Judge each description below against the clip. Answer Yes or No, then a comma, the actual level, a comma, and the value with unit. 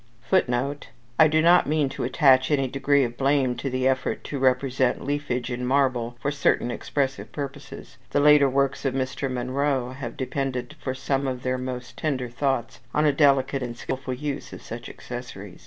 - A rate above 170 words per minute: Yes, average, 180 wpm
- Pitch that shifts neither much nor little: No, narrow, 2.0 semitones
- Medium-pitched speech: No, low, 130 Hz